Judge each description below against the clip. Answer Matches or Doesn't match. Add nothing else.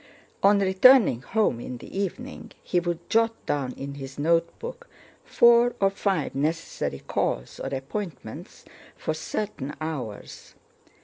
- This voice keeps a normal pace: Doesn't match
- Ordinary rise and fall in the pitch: Doesn't match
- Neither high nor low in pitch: Matches